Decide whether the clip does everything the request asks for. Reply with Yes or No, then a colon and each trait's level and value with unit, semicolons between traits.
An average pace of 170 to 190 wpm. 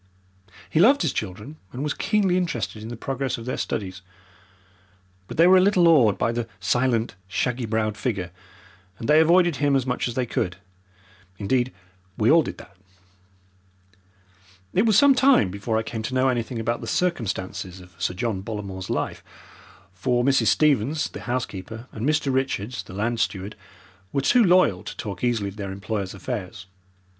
Yes: average, 175 wpm